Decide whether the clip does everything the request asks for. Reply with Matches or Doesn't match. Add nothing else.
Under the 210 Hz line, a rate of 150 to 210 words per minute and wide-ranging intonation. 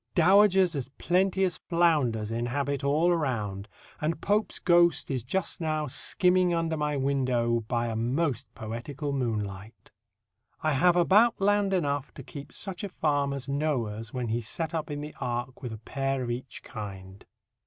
Matches